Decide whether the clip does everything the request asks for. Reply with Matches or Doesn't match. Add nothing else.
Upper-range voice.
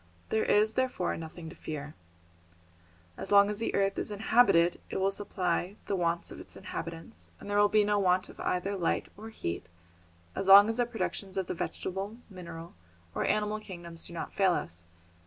Matches